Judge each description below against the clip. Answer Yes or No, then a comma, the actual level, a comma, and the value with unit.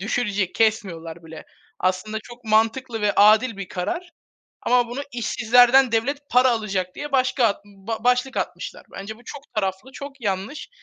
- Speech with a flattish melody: No, average, 4.1 semitones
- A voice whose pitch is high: Yes, high, 225 Hz